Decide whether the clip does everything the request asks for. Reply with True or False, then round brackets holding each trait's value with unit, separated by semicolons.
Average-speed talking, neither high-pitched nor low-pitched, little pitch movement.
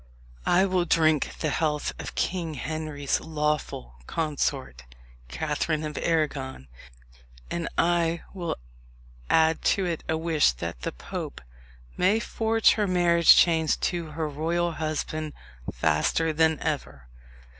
False (125 wpm; 160 Hz; 2.2 semitones)